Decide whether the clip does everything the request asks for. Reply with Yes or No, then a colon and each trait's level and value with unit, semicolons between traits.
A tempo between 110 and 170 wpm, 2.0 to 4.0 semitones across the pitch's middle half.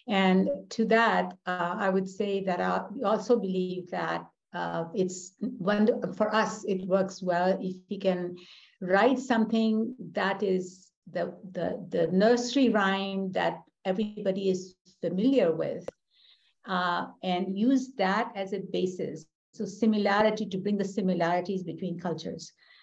Yes: slow, 135 wpm; average, 2.8 semitones